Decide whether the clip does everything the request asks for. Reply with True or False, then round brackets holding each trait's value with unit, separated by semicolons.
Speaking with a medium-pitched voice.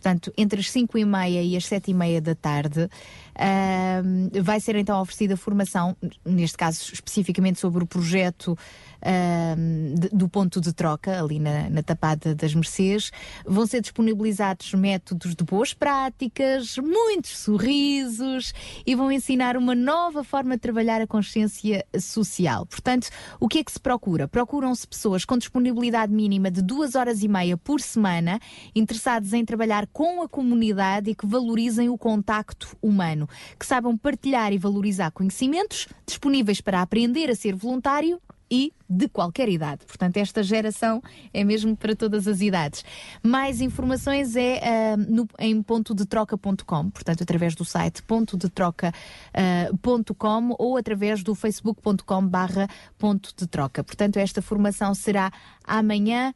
False (210 Hz)